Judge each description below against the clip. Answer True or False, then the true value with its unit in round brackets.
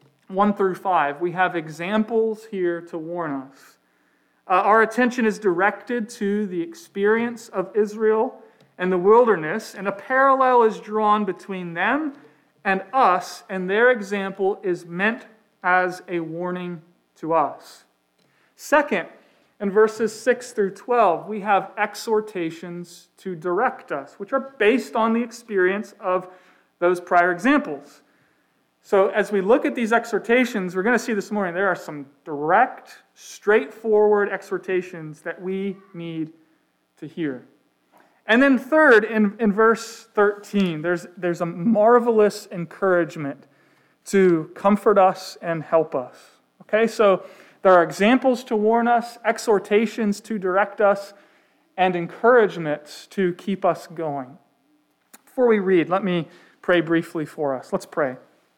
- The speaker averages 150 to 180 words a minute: False (140 wpm)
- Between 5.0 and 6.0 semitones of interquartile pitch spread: False (3.8 semitones)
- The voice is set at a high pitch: True (200 Hz)